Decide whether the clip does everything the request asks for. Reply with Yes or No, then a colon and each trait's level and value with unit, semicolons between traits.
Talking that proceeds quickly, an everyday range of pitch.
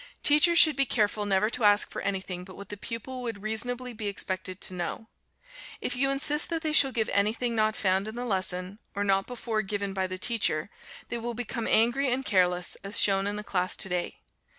Yes: fast, 215 wpm; average, 4.1 semitones